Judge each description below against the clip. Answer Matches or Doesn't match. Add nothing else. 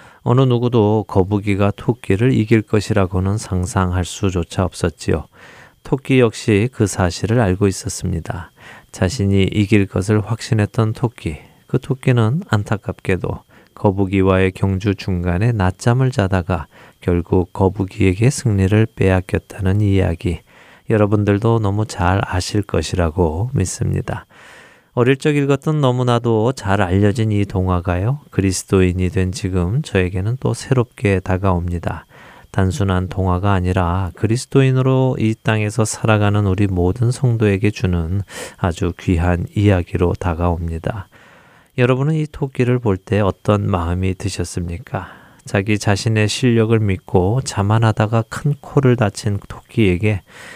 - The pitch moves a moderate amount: Matches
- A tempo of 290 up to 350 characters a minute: Matches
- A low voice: Matches